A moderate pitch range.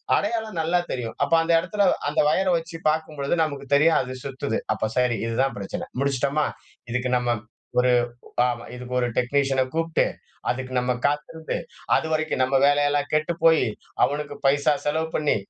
Yes: average, 3.8 semitones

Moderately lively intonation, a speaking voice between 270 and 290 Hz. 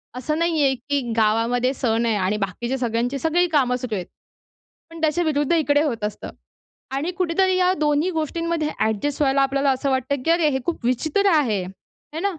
Yes: average, 4.8 semitones; very high, 280 Hz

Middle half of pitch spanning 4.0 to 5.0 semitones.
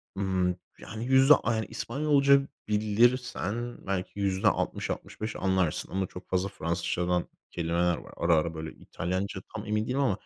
Yes: average, 4.3 semitones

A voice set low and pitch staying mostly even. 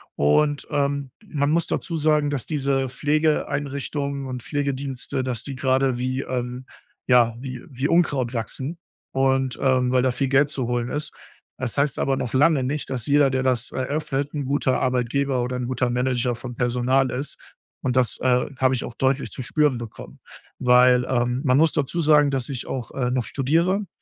Yes: low, 130 Hz; narrow, 2.3 semitones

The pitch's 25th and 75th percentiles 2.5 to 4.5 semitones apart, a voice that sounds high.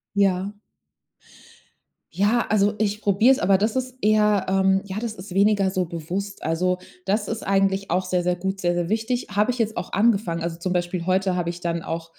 Yes: average, 2.8 semitones; high, 195 Hz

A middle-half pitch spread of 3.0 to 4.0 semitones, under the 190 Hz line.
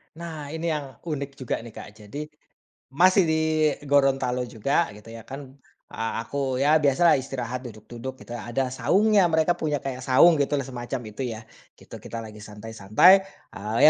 No: average, 4.5 semitones; low, 135 Hz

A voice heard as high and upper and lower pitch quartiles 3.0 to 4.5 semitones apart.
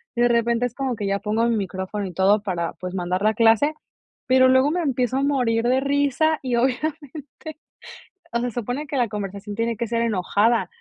Yes: high, 235 Hz; average, 4.2 semitones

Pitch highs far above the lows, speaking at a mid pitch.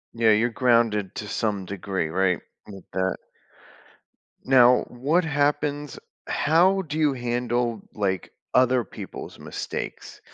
No: wide, 5.7 semitones; low, 120 Hz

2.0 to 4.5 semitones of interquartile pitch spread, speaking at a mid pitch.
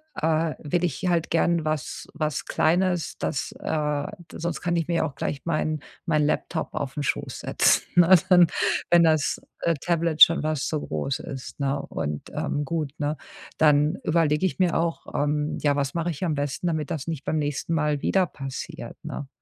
Yes: narrow, 2.5 semitones; medium, 155 Hz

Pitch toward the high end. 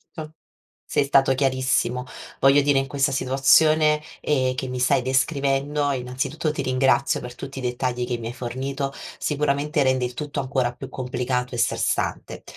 No: low, 135 Hz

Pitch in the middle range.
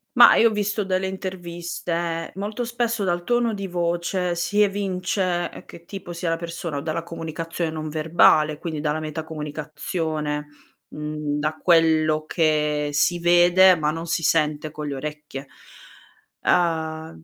Yes: medium, 165 Hz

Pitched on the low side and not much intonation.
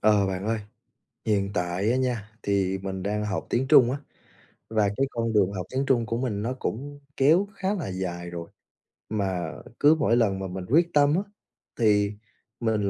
No: low, 110 Hz; average, 5.1 semitones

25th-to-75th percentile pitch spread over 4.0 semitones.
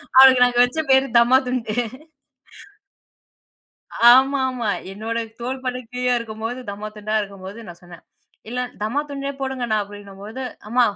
No: average, 3.4 semitones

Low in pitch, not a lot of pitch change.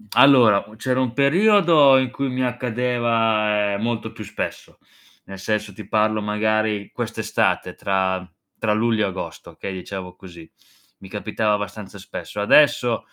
No: low, 110 Hz; average, 3.5 semitones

